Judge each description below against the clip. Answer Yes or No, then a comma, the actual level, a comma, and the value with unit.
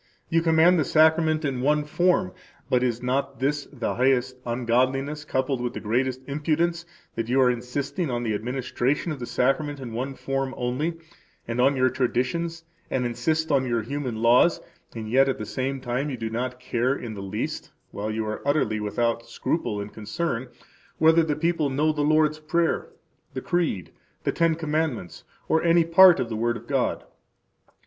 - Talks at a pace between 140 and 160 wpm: No, average, 185 wpm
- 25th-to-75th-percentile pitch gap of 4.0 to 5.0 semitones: Yes, average, 4.3 semitones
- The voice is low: Yes, low, 130 Hz